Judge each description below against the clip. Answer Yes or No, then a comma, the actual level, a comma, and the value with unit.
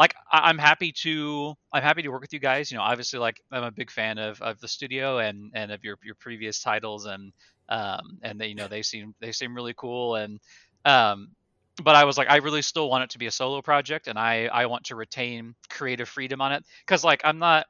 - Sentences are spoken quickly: Yes, fast, 245 wpm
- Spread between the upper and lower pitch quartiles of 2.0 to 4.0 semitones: No, average, 4.8 semitones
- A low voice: Yes, low, 120 Hz